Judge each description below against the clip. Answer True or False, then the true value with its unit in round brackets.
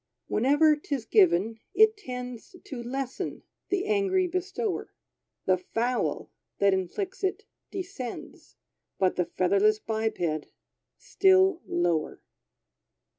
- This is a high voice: True (255 Hz)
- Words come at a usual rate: False (100 wpm)